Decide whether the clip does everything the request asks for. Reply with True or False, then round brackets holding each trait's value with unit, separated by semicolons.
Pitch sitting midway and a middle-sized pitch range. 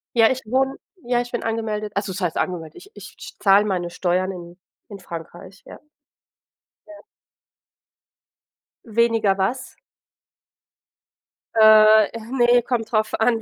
False (215 Hz; 3.6 semitones)